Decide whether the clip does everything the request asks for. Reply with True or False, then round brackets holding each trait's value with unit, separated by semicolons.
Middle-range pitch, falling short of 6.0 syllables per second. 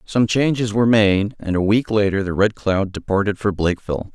False (105 Hz; 5.5 syllables/s)